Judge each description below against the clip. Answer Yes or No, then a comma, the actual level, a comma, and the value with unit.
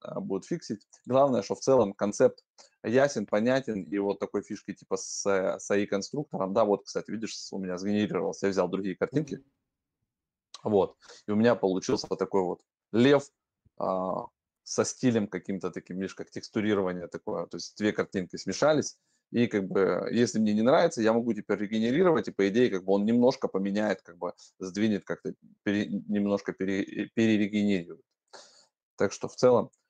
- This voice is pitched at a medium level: No, low, 105 Hz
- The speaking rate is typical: No, fast, 165 wpm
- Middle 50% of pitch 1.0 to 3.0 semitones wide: Yes, average, 2.7 semitones